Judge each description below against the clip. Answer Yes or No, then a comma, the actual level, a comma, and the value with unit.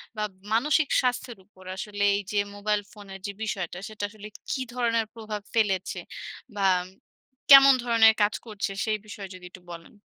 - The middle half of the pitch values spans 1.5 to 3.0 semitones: Yes, narrow, 2.5 semitones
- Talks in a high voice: Yes, high, 210 Hz